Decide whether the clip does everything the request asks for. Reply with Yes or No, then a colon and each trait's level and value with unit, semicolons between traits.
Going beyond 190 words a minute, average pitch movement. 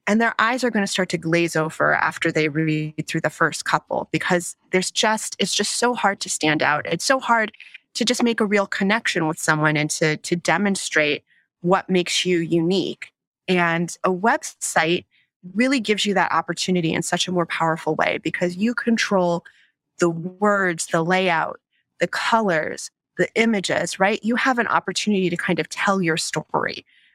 No: average, 180 wpm; average, 3.8 semitones